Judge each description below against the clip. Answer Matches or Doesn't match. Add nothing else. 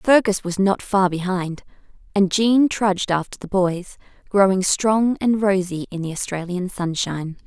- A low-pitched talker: Doesn't match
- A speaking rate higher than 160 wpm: Doesn't match